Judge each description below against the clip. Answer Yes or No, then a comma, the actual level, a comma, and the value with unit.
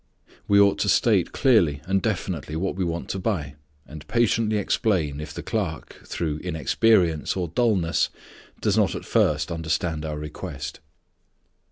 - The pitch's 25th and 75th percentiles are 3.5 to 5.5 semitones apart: Yes, average, 4.7 semitones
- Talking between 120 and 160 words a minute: Yes, average, 150 wpm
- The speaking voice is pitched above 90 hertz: No, very low, 85 Hz